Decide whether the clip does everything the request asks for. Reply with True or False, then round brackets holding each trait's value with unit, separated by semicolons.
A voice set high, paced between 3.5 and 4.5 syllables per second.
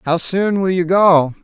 False (180 Hz; 4.0 syllables/s)